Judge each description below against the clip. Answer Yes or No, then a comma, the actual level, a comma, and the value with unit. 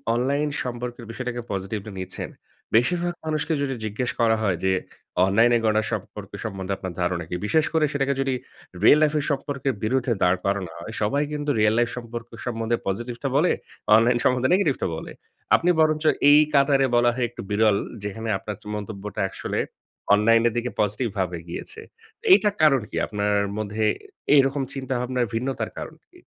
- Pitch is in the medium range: No, low, 120 Hz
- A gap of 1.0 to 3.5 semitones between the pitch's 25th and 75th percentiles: No, average, 4.7 semitones